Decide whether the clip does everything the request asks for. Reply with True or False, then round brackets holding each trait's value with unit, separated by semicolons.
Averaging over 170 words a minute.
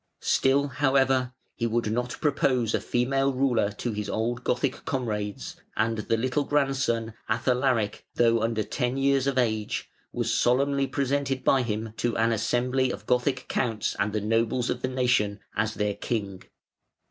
False (160 wpm)